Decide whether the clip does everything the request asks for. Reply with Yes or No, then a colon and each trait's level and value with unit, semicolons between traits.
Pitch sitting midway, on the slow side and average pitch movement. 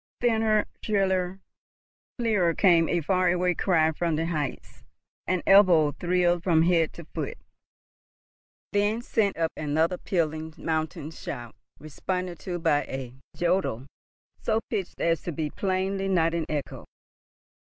Yes: medium, 175 Hz; slow, 130 wpm; average, 3.1 semitones